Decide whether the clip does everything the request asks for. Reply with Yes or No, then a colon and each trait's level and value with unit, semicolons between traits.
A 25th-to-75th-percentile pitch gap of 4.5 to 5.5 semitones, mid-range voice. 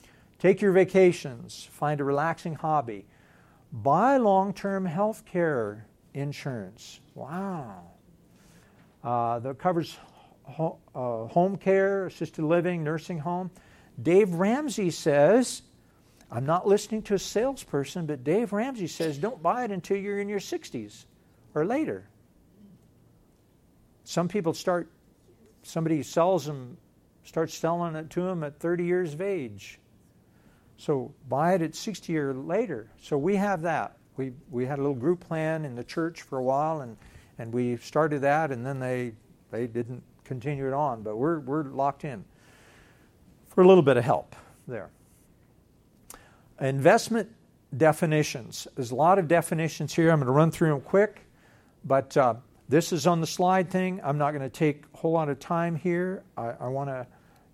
Yes: average, 5.1 semitones; medium, 160 Hz